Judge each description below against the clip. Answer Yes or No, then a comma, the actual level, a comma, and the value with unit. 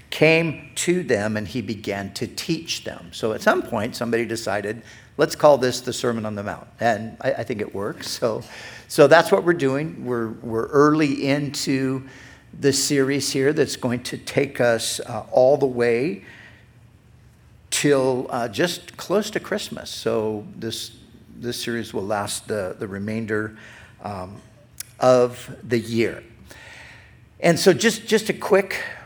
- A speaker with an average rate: Yes, average, 155 wpm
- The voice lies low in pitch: Yes, low, 120 Hz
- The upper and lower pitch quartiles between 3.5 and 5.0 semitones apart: Yes, average, 3.8 semitones